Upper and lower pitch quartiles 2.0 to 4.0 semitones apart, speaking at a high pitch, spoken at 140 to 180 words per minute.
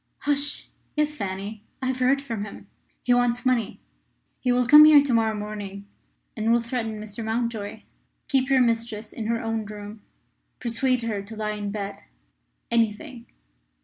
Yes: average, 3.1 semitones; high, 230 Hz; average, 160 wpm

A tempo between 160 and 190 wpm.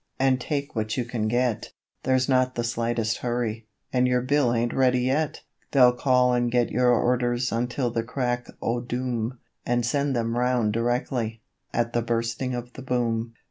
Yes: average, 175 wpm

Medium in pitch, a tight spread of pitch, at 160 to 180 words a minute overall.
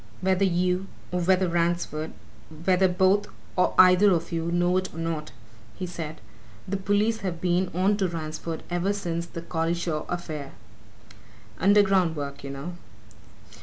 No: medium, 175 Hz; narrow, 2.3 semitones; average, 145 wpm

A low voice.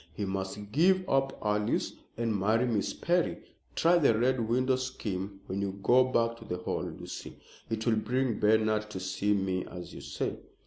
Yes: low, 110 Hz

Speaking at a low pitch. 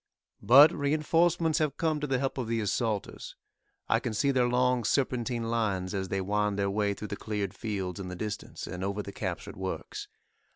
Yes: low, 115 Hz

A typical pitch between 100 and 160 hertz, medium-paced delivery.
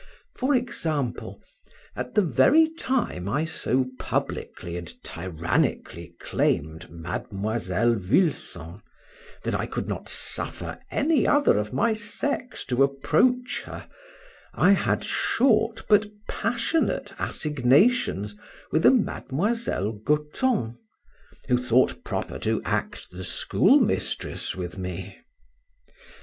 No: low, 135 Hz; slow, 105 wpm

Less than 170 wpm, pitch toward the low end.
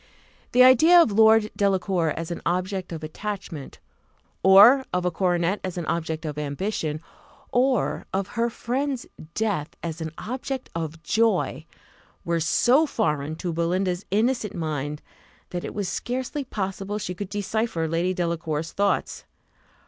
No: average, 140 wpm; medium, 185 Hz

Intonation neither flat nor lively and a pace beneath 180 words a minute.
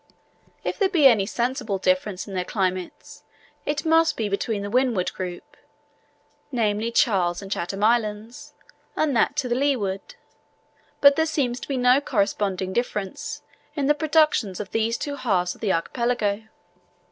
No: wide, 5.7 semitones; average, 150 wpm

